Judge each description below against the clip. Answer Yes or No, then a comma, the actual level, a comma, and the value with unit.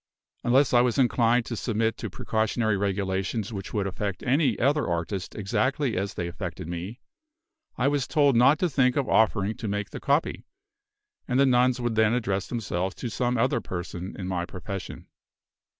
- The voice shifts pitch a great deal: No, average, 4.6 semitones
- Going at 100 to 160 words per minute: No, average, 175 wpm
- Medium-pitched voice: No, low, 115 Hz